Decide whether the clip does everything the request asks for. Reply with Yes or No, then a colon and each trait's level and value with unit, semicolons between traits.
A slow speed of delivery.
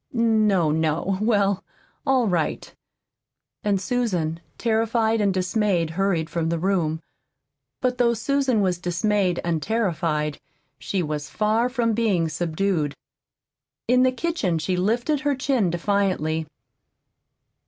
Yes: slow, 120 wpm